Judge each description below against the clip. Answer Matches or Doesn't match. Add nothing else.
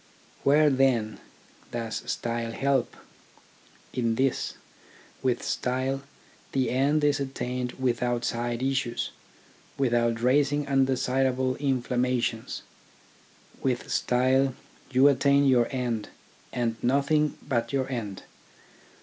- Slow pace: Matches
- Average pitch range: Doesn't match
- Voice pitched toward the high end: Doesn't match